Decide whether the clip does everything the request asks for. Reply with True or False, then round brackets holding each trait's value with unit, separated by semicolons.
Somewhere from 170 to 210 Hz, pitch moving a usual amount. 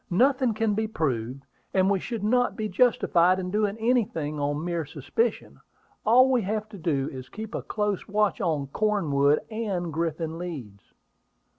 False (190 Hz; 6.1 semitones)